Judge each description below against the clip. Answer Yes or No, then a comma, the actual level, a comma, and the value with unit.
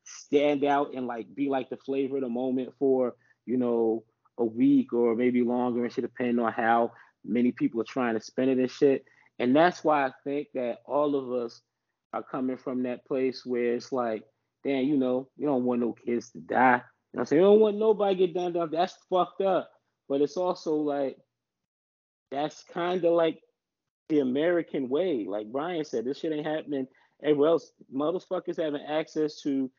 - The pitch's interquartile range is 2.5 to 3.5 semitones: No, average, 3.9 semitones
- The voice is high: No, low, 135 Hz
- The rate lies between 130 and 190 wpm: No, average, 200 wpm